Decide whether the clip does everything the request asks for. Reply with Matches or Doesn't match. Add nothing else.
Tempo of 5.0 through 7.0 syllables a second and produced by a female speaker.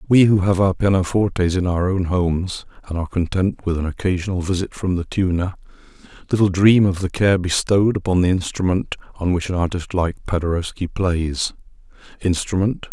Doesn't match